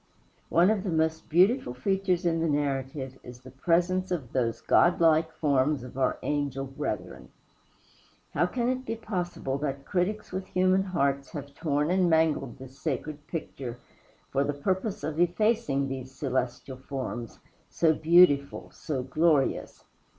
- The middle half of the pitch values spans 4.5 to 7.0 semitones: Yes, average, 4.8 semitones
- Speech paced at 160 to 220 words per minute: No, average, 145 wpm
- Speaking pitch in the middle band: Yes, medium, 150 Hz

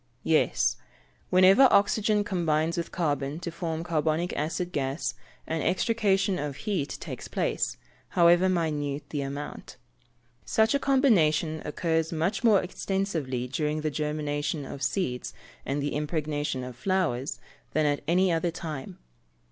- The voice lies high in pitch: No, medium, 160 Hz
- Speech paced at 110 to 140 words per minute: Yes, slow, 135 wpm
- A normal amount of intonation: Yes, average, 4.0 semitones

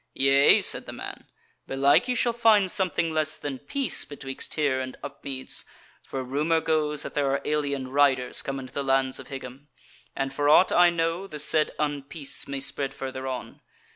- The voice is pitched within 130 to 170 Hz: Yes, medium, 140 Hz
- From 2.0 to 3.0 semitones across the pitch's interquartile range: Yes, average, 2.7 semitones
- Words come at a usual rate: Yes, average, 180 wpm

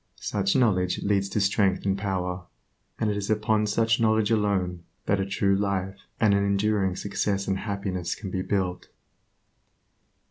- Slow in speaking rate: No, average, 155 wpm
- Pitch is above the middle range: No, low, 100 Hz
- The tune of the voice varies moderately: No, narrow, 1.6 semitones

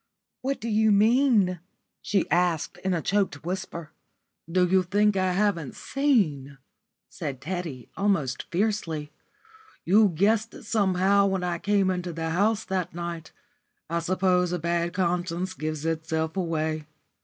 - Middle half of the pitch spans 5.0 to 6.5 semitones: No, average, 3.4 semitones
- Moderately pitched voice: Yes, medium, 180 Hz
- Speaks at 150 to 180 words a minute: No, average, 140 wpm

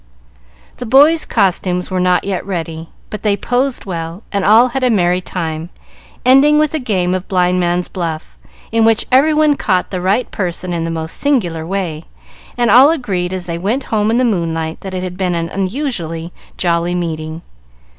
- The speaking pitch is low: No, medium, 185 Hz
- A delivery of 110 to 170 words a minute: No, average, 185 wpm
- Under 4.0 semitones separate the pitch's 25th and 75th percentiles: No, wide, 5.4 semitones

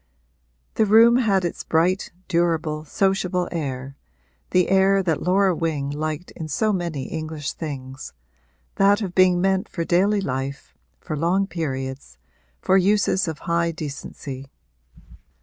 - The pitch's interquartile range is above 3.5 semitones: Yes, average, 4.2 semitones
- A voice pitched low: No, medium, 170 Hz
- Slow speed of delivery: Yes, slow, 130 wpm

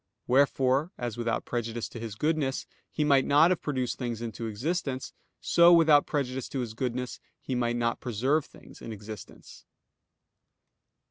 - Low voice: Yes, low, 125 Hz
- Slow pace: No, average, 150 wpm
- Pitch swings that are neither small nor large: Yes, average, 3.6 semitones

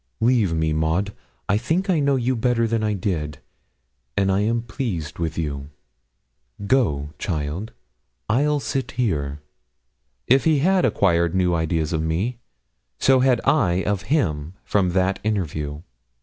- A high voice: No, low, 100 Hz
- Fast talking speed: No, average, 145 wpm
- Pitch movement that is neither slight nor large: No, wide, 7.3 semitones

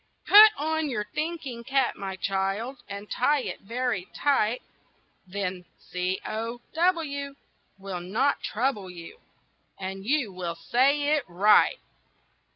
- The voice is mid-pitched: No, high, 230 Hz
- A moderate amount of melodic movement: No, wide, 6.6 semitones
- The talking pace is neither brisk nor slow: No, slow, 125 wpm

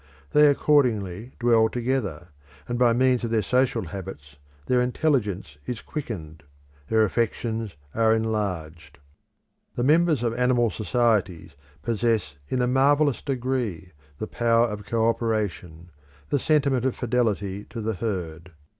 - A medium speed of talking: No, slow, 130 wpm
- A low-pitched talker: Yes, low, 115 Hz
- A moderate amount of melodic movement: Yes, average, 4.2 semitones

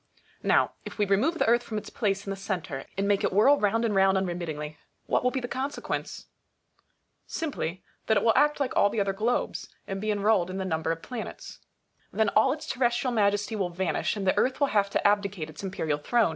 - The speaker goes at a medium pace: No, fast, 225 wpm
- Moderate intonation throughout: Yes, average, 3.7 semitones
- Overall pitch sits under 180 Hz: No, high, 205 Hz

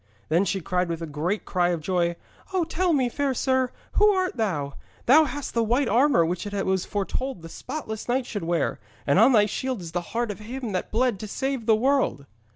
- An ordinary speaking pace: No, fast, 225 wpm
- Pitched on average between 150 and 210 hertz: No, high, 220 Hz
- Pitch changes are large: Yes, wide, 6.8 semitones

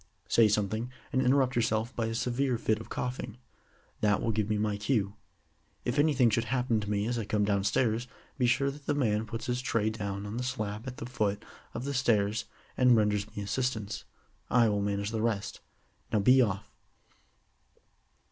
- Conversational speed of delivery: Yes, average, 185 wpm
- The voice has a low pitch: Yes, low, 115 Hz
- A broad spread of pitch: No, average, 3.1 semitones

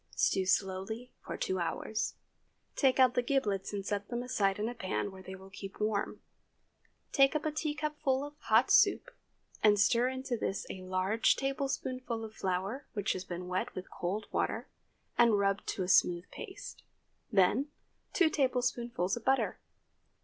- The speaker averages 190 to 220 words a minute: No, average, 165 wpm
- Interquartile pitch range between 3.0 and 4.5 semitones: No, average, 5.2 semitones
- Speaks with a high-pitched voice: Yes, high, 220 Hz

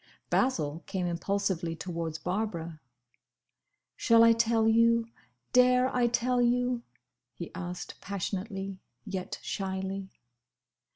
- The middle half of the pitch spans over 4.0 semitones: Yes, average, 4.4 semitones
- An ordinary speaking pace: No, slow, 100 wpm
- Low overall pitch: No, high, 195 Hz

